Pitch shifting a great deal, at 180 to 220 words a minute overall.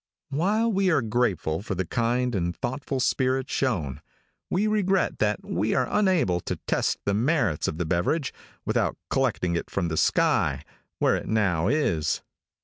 No: wide, 8.6 semitones; average, 160 wpm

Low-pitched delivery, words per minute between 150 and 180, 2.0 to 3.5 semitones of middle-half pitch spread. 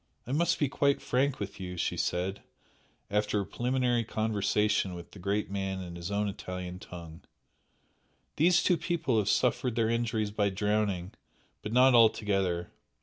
No: low, 105 Hz; average, 155 wpm; average, 4.1 semitones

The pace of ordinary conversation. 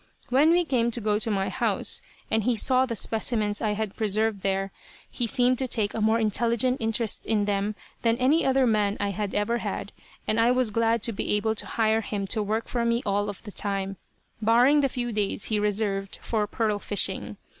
No: fast, 210 wpm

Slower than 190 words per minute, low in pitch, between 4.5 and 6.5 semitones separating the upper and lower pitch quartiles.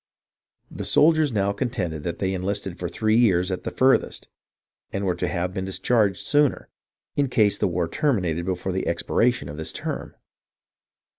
Yes: average, 165 wpm; very low, 95 Hz; average, 5.1 semitones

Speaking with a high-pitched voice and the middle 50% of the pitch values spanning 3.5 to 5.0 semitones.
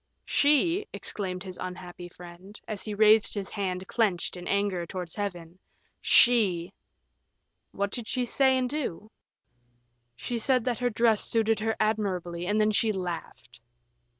Yes: high, 205 Hz; average, 3.9 semitones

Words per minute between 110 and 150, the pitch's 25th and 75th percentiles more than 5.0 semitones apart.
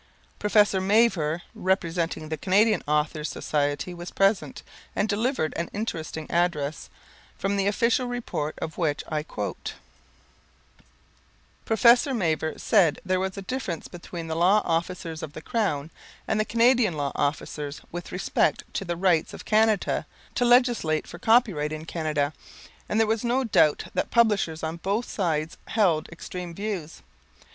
Yes: average, 145 wpm; wide, 5.4 semitones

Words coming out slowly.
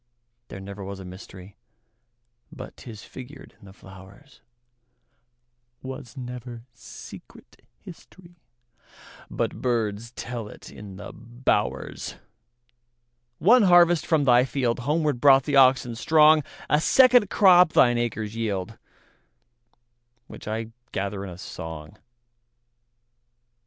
Yes: slow, 90 wpm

